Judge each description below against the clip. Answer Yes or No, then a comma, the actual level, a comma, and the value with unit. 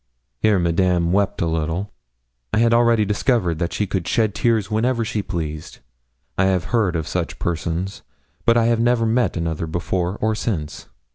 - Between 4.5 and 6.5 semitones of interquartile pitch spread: Yes, average, 5.0 semitones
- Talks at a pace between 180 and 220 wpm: No, average, 165 wpm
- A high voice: No, very low, 95 Hz